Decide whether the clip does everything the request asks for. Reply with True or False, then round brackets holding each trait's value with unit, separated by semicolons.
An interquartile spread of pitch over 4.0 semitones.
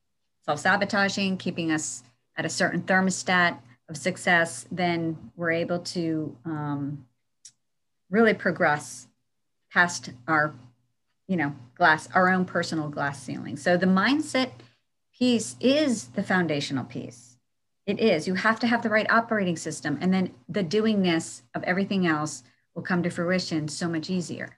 True (4.4 semitones)